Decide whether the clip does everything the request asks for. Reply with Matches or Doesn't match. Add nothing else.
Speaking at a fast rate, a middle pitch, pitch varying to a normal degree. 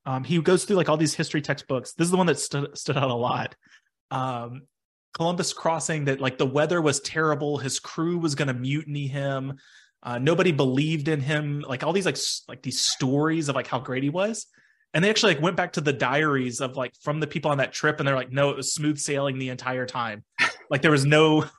Matches